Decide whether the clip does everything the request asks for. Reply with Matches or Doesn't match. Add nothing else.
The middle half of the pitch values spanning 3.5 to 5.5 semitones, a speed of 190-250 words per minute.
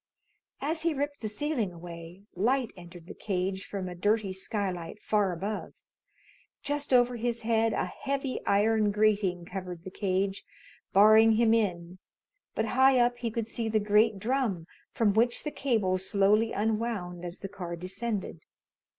Doesn't match